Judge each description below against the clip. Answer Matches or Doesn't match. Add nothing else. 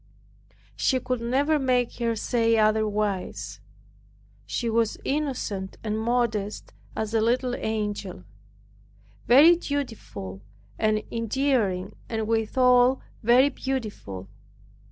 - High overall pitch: Matches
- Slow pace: Matches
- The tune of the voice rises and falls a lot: Doesn't match